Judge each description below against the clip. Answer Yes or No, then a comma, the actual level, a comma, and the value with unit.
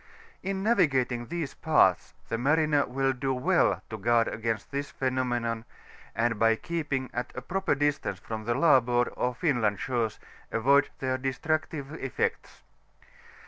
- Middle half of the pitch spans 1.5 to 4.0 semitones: Yes, average, 3.7 semitones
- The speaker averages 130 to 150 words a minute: Yes, average, 140 wpm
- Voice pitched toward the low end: Yes, low, 130 Hz